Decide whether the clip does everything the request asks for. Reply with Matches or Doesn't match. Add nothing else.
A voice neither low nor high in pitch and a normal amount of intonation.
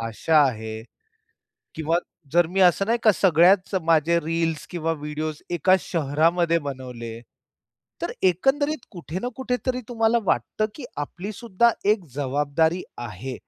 Matches